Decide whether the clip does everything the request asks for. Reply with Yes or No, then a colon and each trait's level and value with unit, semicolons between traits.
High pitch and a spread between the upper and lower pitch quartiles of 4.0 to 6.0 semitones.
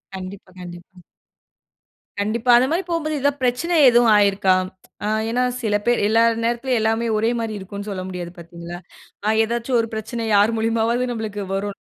No: high, 220 Hz; average, 3.2 semitones